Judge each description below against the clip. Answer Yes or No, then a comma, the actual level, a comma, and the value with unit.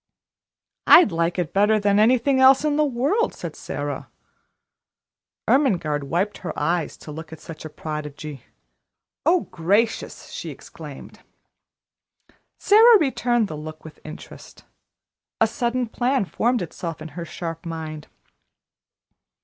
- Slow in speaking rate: Yes, slow, 125 wpm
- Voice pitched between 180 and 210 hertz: Yes, high, 190 Hz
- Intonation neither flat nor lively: No, wide, 8.0 semitones